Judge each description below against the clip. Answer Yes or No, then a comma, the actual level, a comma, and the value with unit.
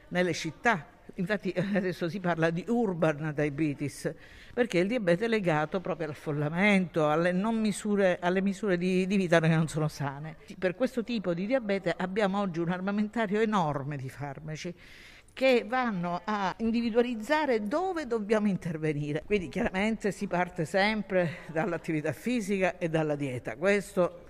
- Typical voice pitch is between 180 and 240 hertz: Yes, medium, 185 Hz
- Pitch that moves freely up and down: No, average, 4.4 semitones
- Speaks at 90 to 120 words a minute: No, average, 145 wpm